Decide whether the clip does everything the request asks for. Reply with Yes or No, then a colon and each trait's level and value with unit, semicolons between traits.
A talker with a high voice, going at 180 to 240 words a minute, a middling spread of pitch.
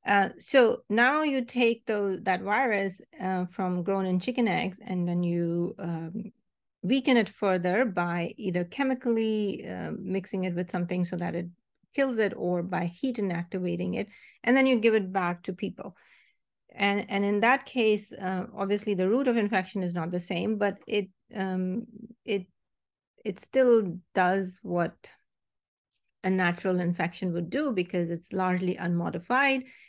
No: high, 195 Hz; average, 160 wpm; average, 4.0 semitones